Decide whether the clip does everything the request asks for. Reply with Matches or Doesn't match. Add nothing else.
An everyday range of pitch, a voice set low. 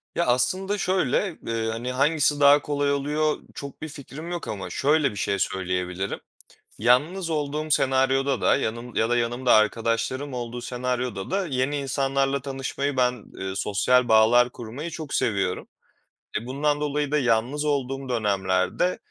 Matches